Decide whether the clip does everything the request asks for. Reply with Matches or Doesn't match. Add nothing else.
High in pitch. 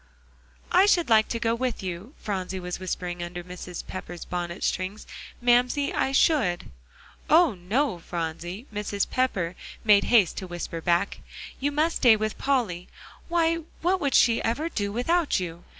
Matches